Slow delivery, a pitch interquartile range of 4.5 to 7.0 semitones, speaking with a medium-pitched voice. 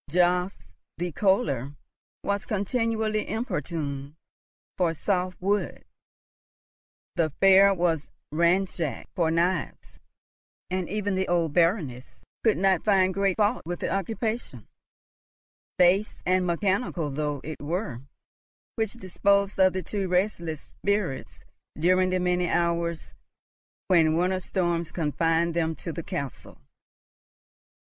No: slow, 115 wpm; average, 3.1 semitones; medium, 180 Hz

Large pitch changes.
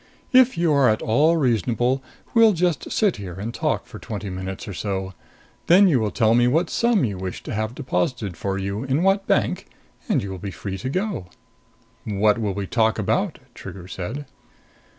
Yes: wide, 7.7 semitones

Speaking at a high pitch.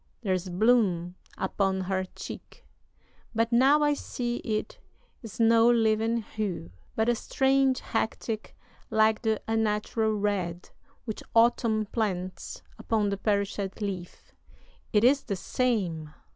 Yes: high, 215 Hz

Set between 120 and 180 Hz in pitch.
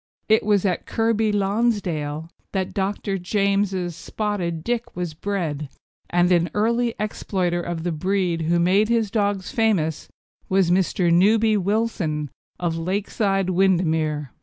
No: high, 190 Hz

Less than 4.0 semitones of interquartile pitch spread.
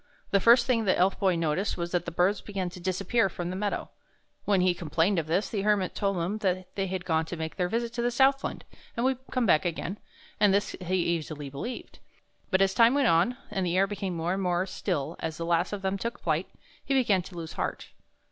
Yes: average, 3.3 semitones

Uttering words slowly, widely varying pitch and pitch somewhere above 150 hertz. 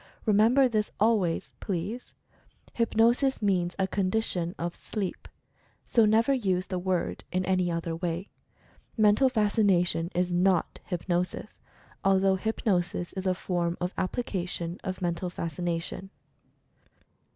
No: slow, 125 wpm; average, 3.3 semitones; medium, 185 Hz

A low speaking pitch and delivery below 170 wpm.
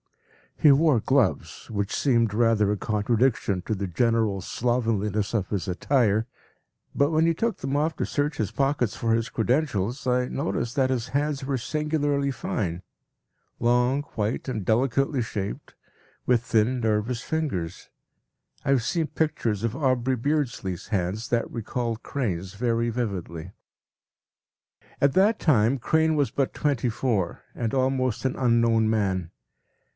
Yes: low, 120 Hz; average, 140 wpm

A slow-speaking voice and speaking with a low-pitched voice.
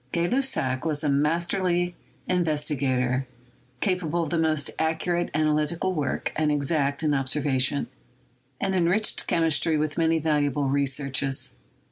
No: slow, 120 wpm; medium, 155 Hz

